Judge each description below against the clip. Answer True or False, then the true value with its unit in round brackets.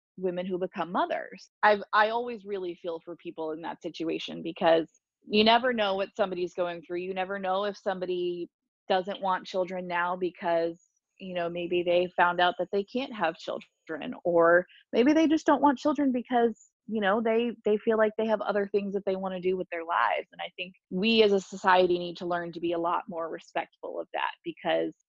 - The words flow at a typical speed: False (210 wpm)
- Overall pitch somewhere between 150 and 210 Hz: True (185 Hz)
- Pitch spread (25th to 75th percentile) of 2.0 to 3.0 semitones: False (3.5 semitones)